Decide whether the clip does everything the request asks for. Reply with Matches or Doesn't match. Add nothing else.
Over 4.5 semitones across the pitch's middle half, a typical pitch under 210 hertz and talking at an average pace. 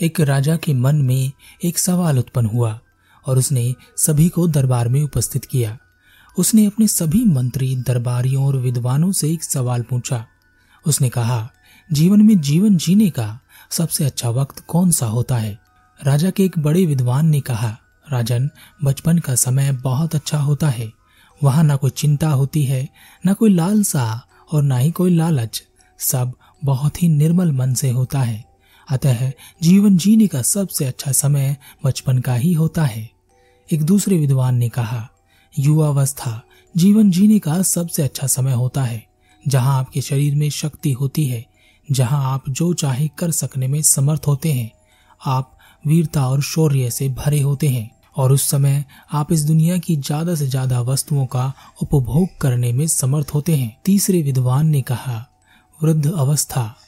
Doesn't match